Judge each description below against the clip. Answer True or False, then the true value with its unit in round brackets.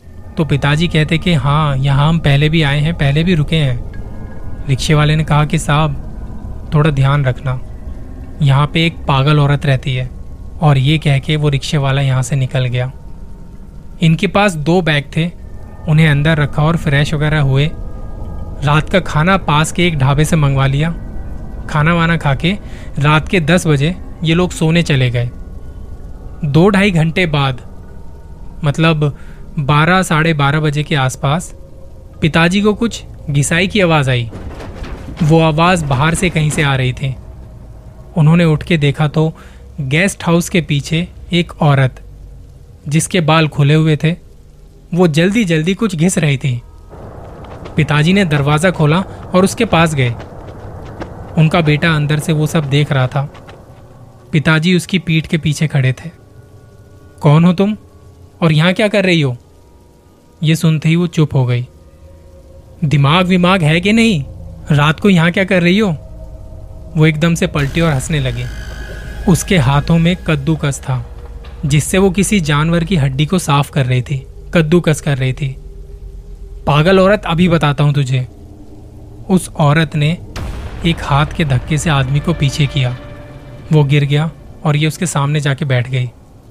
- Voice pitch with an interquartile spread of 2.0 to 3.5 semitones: False (4.7 semitones)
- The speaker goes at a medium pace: True (160 wpm)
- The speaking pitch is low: False (150 Hz)